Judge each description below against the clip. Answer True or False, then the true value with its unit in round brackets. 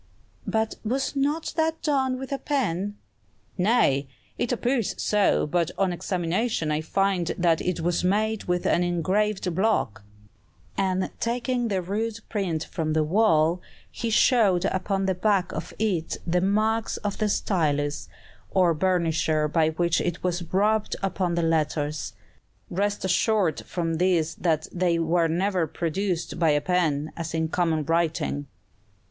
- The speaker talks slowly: False (145 wpm)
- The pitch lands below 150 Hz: False (180 Hz)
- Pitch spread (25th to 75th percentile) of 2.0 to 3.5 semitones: False (4.3 semitones)